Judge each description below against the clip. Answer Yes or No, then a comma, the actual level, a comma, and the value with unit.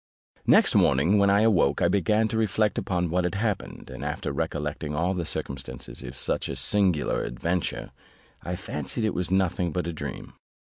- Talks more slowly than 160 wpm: No, average, 180 wpm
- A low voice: Yes, very low, 90 Hz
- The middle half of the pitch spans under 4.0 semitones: No, average, 5.0 semitones